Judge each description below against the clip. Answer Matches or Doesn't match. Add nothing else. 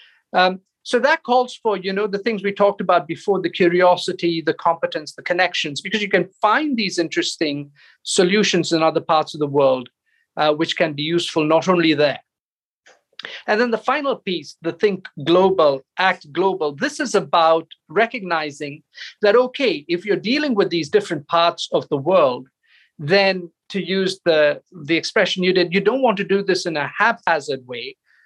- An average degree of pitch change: Matches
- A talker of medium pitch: Matches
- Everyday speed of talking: Matches